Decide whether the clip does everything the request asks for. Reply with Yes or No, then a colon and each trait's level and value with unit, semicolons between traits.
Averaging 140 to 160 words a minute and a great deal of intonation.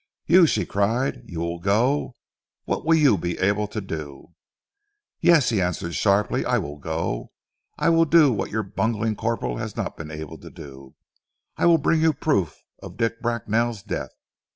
No: average, 175 wpm; wide, 7.3 semitones